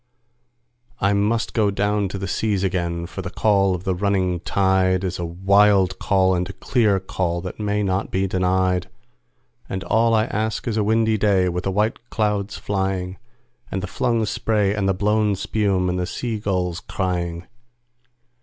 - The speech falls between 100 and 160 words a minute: No, average, 175 wpm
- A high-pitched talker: No, very low, 95 Hz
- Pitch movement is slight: Yes, narrow, 2.2 semitones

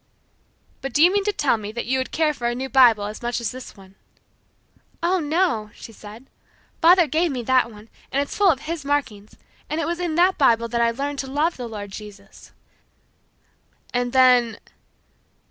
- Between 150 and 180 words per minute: No, average, 195 wpm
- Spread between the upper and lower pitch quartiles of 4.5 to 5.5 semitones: Yes, average, 5.2 semitones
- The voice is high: Yes, very high, 260 Hz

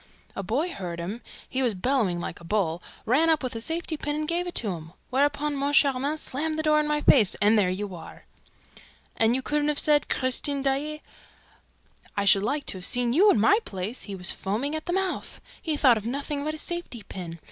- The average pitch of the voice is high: Yes, very high, 265 Hz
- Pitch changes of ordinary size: No, wide, 6.7 semitones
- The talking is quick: Yes, fast, 220 wpm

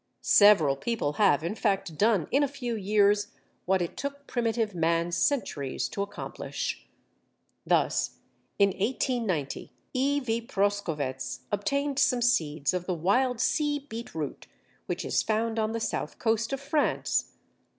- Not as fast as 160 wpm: Yes, average, 140 wpm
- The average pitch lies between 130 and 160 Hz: No, high, 210 Hz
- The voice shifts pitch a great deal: Yes, wide, 6.1 semitones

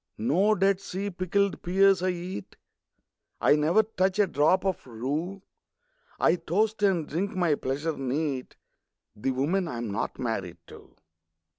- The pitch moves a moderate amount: No, wide, 5.8 semitones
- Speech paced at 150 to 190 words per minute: No, average, 140 wpm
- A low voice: No, medium, 175 Hz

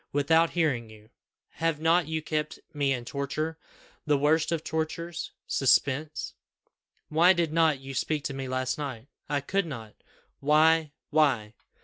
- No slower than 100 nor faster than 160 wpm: Yes, average, 145 wpm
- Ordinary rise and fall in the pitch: Yes, average, 3.0 semitones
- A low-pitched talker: No, medium, 150 Hz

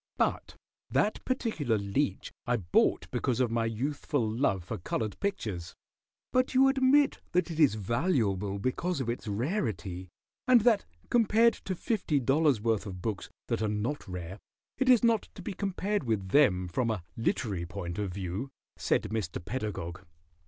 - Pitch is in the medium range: No, low, 115 Hz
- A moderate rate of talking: Yes, average, 160 wpm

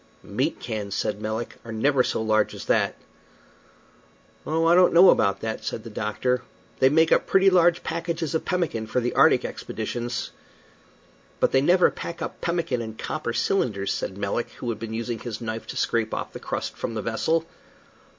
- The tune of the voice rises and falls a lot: Yes, wide, 6.8 semitones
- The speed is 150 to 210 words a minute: Yes, average, 185 wpm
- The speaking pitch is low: Yes, low, 120 Hz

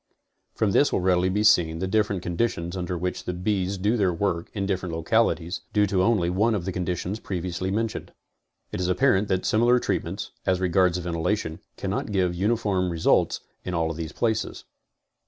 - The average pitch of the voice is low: Yes, very low, 95 Hz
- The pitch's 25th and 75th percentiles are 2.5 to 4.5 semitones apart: Yes, average, 3.0 semitones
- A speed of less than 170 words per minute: No, average, 175 wpm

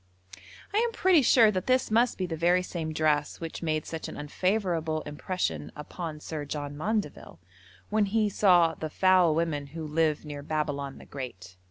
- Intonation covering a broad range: No, average, 4.1 semitones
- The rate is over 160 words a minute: Yes, average, 175 wpm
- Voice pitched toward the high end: No, medium, 160 Hz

